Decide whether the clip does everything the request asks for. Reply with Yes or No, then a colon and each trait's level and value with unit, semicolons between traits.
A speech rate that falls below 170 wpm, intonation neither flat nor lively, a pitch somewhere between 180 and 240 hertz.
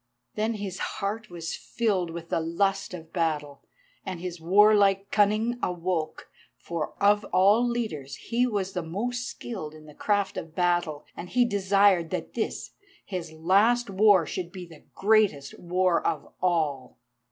Yes: average, 155 wpm; average, 3.9 semitones; medium, 185 Hz